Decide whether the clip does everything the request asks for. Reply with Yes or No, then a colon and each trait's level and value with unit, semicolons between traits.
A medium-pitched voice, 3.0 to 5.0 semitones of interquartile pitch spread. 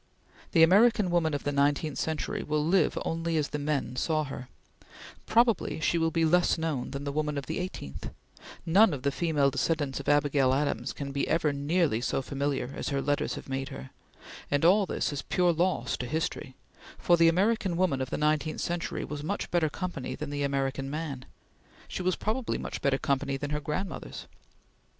Yes: medium, 150 Hz; average, 3.4 semitones